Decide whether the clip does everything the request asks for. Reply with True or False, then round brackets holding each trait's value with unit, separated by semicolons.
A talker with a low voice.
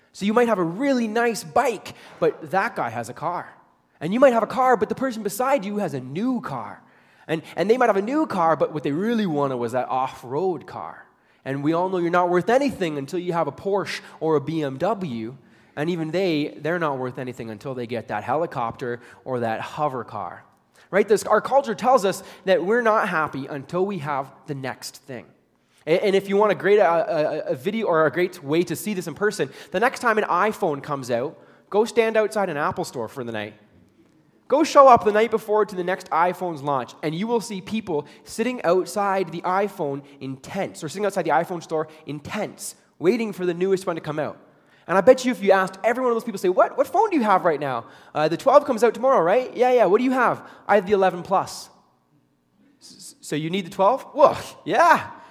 False (180 Hz)